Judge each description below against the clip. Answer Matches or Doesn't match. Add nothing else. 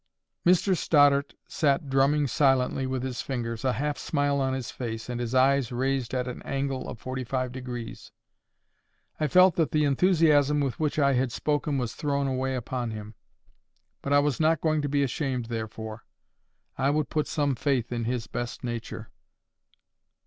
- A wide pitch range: Doesn't match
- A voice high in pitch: Doesn't match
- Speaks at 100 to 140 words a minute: Doesn't match